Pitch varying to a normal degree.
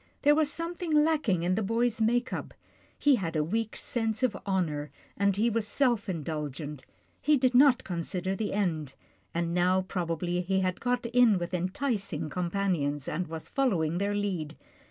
No: wide, 5.8 semitones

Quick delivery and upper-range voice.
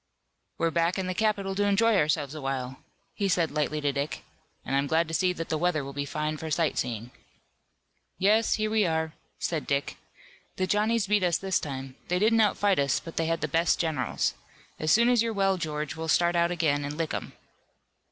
No: fast, 210 wpm; medium, 165 Hz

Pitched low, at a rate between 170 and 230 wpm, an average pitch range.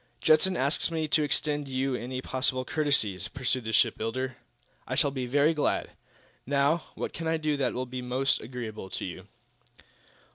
Yes: low, 130 Hz; average, 175 wpm; average, 3.0 semitones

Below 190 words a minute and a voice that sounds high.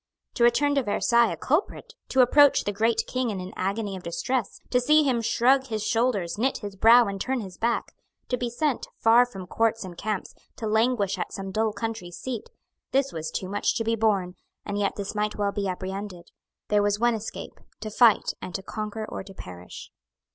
No: fast, 205 wpm; high, 220 Hz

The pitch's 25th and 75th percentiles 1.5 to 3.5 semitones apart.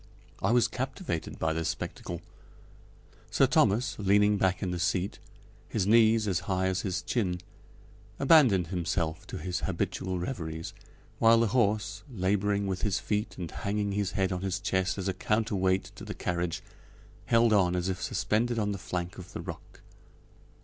Yes: average, 2.9 semitones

